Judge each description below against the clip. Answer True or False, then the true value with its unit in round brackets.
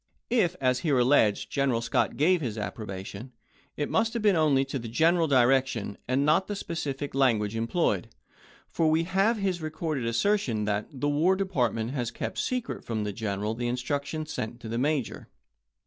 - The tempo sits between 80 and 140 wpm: False (185 wpm)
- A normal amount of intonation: False (5.9 semitones)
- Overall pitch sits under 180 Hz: True (135 Hz)